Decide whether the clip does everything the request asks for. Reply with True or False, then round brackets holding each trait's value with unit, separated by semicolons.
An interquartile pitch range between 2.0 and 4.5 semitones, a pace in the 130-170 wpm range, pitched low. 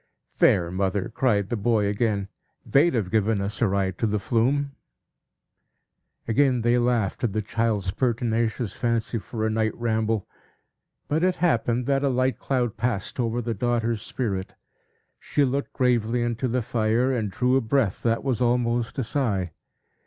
True (2.7 semitones; 160 wpm; 115 Hz)